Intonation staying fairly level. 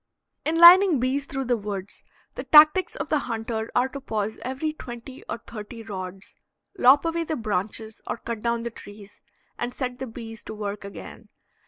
No: average, 4.3 semitones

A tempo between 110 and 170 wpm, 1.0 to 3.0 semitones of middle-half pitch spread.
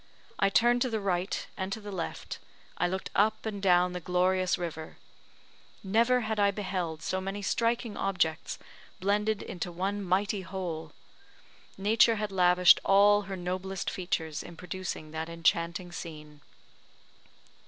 Yes: average, 145 wpm; narrow, 2.6 semitones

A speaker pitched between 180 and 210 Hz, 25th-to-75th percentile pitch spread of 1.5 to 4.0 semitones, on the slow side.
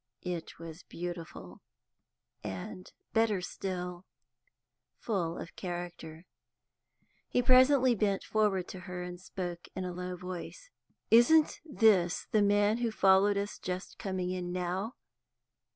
Yes: medium, 185 Hz; average, 3.1 semitones; slow, 120 wpm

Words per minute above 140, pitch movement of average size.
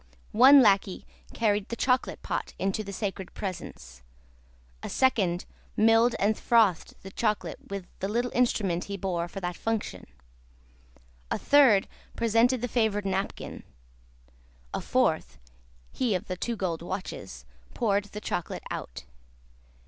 No: slow, 135 wpm; average, 3.6 semitones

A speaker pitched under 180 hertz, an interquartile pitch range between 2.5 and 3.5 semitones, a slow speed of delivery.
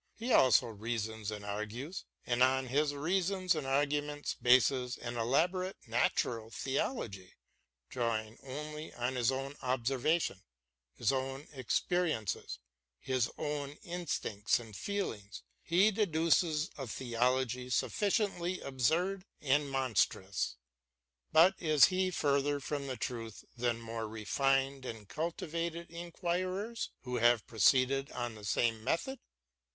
No: low, 135 Hz; wide, 5.6 semitones; slow, 120 wpm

